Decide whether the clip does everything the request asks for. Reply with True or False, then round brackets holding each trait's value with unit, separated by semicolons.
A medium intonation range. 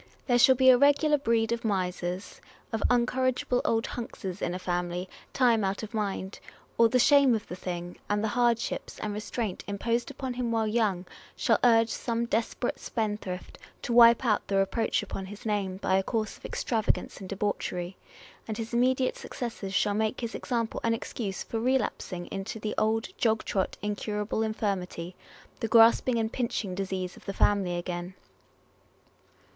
True (3.4 semitones)